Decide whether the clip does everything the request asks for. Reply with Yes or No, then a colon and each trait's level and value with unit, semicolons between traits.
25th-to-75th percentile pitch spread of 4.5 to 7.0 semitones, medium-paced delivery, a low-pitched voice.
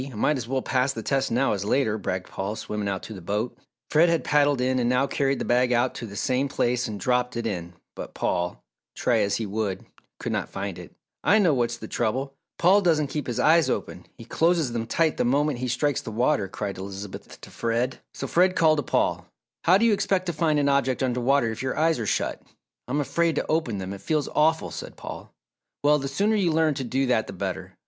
No: average, 5.2 semitones; fast, 235 wpm; low, 130 Hz